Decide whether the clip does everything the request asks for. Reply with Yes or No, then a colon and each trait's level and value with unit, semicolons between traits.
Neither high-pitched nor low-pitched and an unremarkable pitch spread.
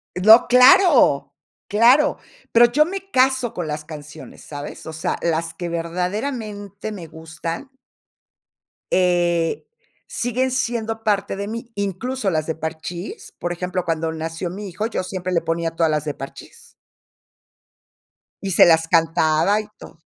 No: medium, 180 Hz; wide, 5.8 semitones